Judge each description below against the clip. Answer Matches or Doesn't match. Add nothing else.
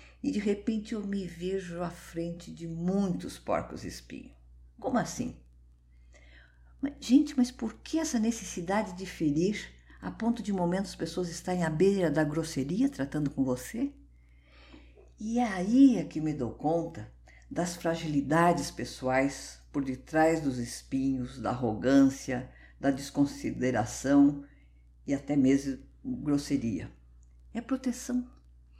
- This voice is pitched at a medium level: Matches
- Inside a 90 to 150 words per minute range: Matches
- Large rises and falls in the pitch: Matches